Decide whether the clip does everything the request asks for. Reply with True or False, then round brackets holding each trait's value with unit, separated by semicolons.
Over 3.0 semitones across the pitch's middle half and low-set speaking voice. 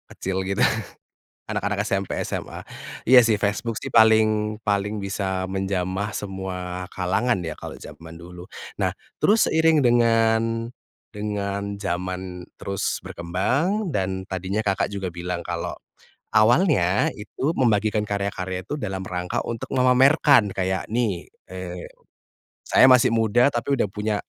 True (3.5 semitones; 100 Hz)